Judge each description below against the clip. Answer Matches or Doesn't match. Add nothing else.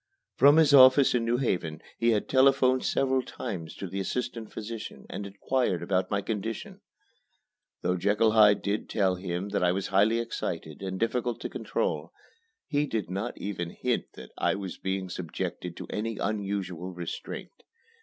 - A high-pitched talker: Doesn't match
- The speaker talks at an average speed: Matches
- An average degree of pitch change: Matches